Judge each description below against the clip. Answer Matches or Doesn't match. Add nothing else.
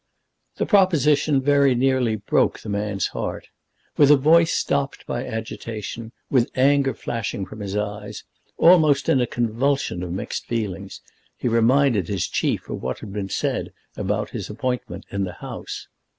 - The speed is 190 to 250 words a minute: Doesn't match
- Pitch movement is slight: Doesn't match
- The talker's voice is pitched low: Matches